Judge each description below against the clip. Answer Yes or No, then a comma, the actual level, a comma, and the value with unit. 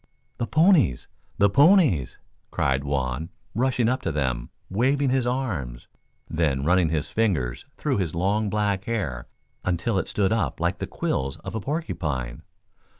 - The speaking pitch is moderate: No, very low, 95 Hz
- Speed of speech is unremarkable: Yes, average, 150 wpm